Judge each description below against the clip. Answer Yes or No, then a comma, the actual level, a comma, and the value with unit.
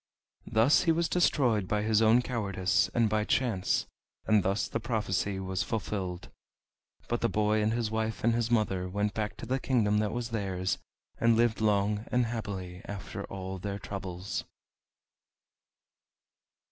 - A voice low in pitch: Yes, low, 105 Hz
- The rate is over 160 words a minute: No, average, 155 wpm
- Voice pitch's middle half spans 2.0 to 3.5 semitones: Yes, average, 3.1 semitones